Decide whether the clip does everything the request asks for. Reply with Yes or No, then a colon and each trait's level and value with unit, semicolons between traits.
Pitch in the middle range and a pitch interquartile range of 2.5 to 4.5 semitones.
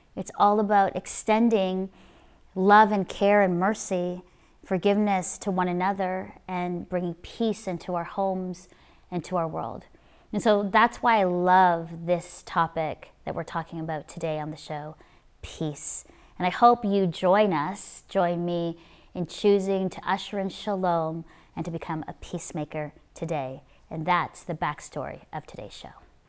Yes: medium, 180 Hz; average, 2.9 semitones